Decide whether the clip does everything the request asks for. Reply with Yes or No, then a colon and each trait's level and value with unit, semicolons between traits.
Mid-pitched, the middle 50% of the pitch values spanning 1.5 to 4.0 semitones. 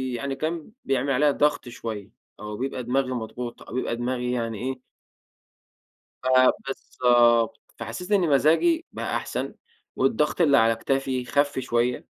No: low, 130 Hz; average, 3.1 semitones